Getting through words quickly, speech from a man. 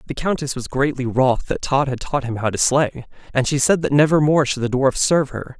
Yes: fast, 255 wpm; male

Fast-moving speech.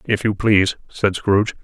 No: average, 185 wpm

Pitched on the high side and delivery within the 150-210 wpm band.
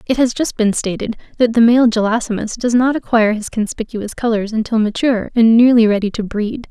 Yes: high, 225 Hz; average, 195 wpm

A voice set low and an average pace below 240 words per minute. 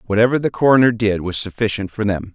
Yes: low, 110 Hz; fast, 205 wpm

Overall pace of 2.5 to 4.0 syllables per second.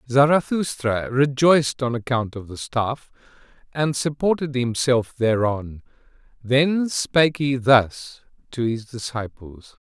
Yes: 3.8 syllables/s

